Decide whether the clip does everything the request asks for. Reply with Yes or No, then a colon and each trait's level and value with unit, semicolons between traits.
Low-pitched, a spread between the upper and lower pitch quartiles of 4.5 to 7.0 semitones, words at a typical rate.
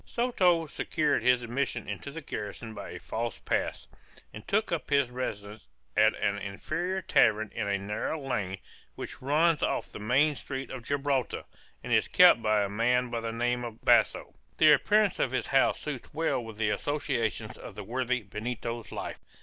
Yes: low, 125 Hz; average, 5.0 semitones; average, 180 wpm